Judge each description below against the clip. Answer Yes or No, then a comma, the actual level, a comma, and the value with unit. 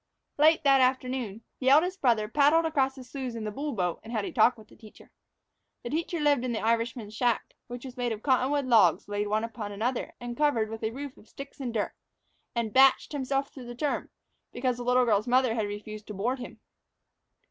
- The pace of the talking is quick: Yes, fast, 220 wpm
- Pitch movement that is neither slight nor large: Yes, average, 3.6 semitones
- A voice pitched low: No, high, 245 Hz